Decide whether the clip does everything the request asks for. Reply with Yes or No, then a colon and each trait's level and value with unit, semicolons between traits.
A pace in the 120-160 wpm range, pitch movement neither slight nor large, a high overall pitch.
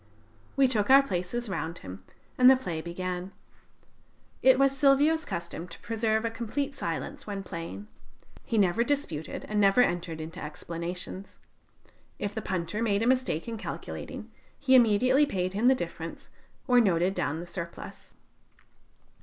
No: average, 150 wpm; wide, 6.4 semitones; high, 205 Hz